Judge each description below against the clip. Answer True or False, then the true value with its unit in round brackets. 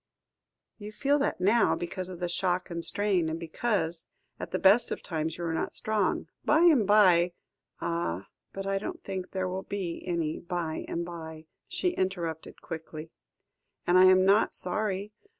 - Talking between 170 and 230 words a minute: True (175 wpm)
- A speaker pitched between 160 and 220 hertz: True (185 Hz)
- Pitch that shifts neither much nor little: True (3.2 semitones)